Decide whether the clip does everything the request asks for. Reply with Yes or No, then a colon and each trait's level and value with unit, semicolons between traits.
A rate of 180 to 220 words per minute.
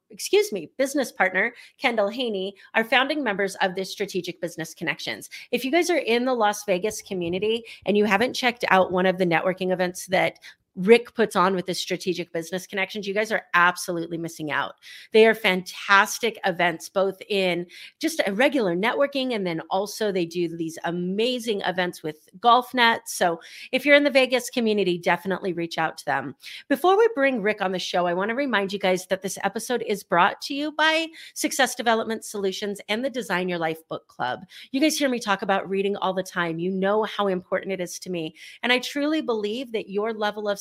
Yes: fast, 205 wpm